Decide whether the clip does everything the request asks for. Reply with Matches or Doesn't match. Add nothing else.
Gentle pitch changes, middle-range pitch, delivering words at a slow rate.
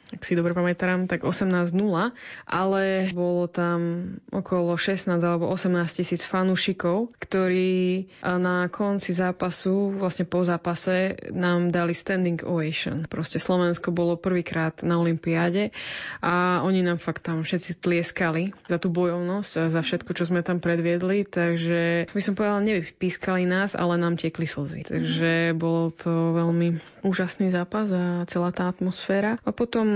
Doesn't match